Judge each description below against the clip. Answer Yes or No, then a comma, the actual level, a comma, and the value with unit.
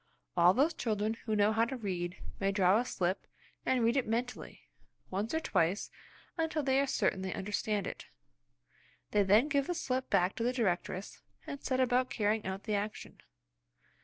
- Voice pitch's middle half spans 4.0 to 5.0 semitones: Yes, average, 4.7 semitones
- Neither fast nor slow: Yes, average, 180 wpm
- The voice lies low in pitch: No, high, 220 Hz